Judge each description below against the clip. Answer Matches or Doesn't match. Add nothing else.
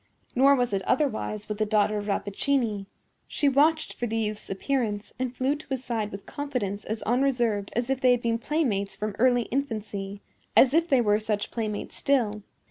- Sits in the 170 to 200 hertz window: Doesn't match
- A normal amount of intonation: Matches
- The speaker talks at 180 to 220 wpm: Matches